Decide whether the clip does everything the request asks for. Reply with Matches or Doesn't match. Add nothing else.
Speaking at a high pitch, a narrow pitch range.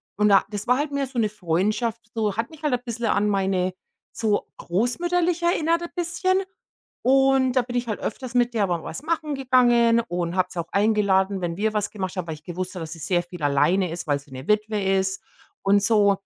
Doesn't match